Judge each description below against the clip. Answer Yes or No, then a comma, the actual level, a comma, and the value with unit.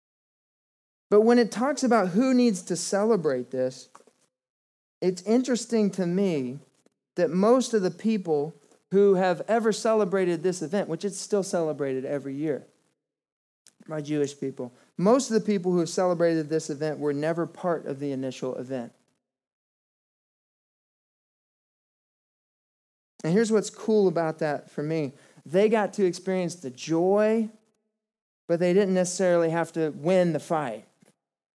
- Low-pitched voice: No, medium, 180 Hz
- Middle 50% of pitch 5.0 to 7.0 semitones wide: Yes, wide, 5.4 semitones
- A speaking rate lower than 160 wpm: Yes, average, 140 wpm